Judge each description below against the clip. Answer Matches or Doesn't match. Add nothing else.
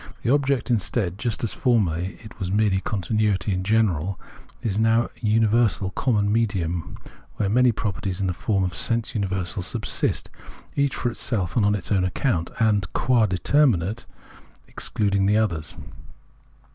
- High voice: Doesn't match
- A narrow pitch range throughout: Doesn't match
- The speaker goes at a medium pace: Matches